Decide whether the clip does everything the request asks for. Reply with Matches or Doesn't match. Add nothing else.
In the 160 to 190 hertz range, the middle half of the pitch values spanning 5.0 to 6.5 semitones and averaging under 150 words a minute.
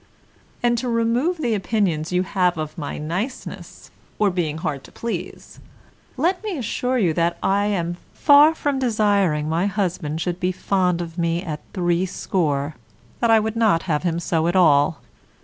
Doesn't match